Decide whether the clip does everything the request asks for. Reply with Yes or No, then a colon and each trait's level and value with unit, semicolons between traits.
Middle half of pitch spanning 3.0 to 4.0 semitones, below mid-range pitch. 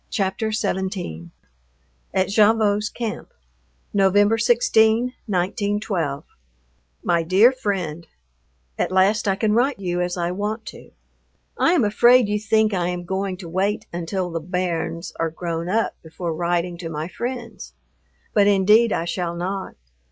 No: average, 3.6 semitones; high, 190 Hz